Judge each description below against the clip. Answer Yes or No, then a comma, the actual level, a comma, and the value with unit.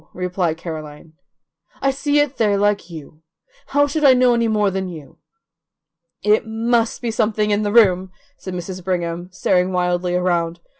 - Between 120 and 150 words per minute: No, average, 160 wpm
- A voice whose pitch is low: No, high, 190 Hz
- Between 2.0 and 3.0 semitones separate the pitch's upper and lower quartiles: No, average, 4.3 semitones